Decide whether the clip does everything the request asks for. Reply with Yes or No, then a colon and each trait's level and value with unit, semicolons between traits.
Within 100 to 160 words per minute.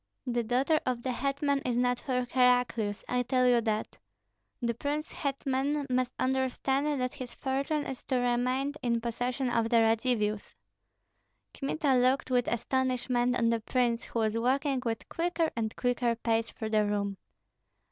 Yes: average, 155 wpm